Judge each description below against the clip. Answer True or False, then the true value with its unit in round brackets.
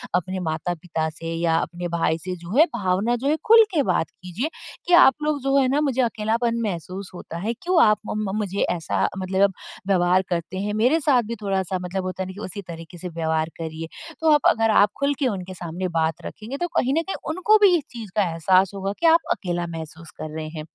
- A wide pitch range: True (5.7 semitones)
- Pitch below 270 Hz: True (190 Hz)